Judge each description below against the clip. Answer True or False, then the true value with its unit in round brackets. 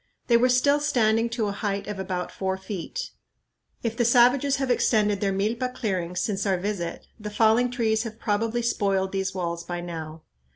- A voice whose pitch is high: True (210 Hz)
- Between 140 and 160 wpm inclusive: False (180 wpm)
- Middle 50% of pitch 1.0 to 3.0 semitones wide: False (3.7 semitones)